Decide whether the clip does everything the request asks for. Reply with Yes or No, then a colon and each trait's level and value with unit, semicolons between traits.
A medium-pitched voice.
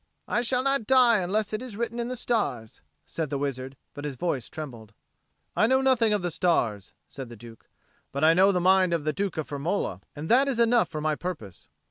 Yes: medium, 175 Hz